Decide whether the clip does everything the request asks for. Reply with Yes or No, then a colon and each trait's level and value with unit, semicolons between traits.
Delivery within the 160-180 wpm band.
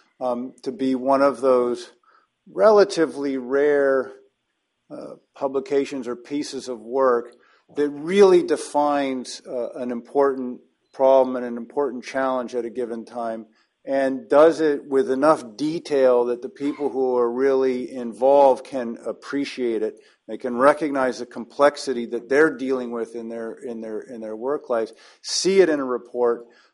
No: average, 150 wpm